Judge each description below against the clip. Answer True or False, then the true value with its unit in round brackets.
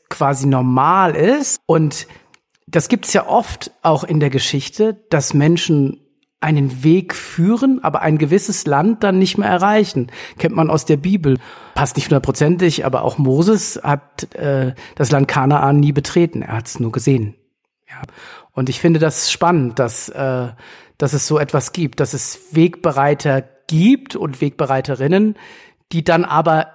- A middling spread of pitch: True (4.2 semitones)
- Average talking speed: True (160 wpm)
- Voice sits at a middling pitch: True (150 Hz)